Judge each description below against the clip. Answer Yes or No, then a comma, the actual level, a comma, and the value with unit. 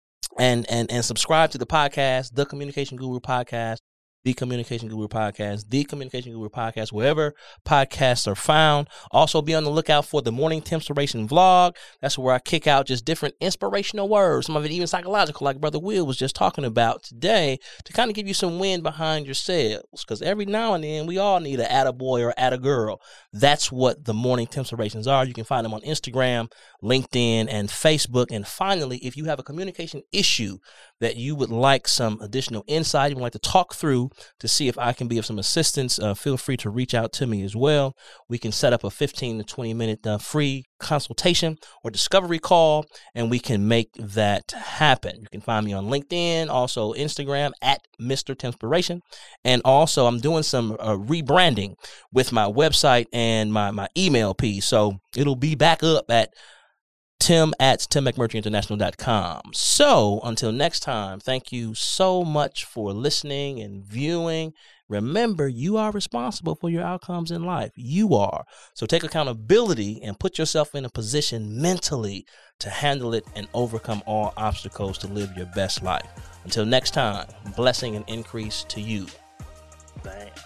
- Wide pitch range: Yes, wide, 5.7 semitones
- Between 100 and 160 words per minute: No, average, 180 wpm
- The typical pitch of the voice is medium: No, low, 130 Hz